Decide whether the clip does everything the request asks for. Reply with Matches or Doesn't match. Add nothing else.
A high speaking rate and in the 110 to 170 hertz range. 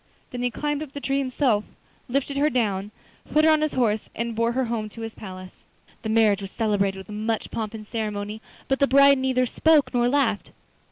Doesn't match